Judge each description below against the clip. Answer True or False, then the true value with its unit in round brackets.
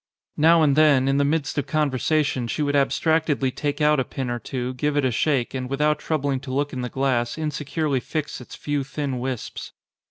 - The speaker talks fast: True (215 wpm)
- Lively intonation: False (2.6 semitones)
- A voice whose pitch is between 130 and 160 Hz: True (140 Hz)